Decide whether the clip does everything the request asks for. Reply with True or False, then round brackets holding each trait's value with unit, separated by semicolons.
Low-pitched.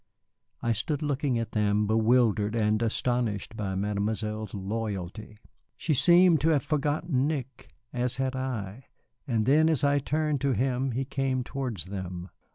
True (120 Hz)